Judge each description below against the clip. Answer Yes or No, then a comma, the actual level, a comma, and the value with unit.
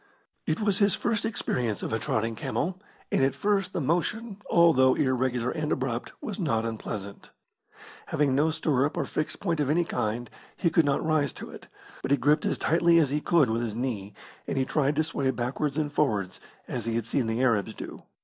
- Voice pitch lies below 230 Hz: Yes, medium, 140 Hz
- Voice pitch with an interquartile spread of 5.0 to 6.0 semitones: Yes, wide, 5.5 semitones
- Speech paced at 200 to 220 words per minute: Yes, fast, 205 wpm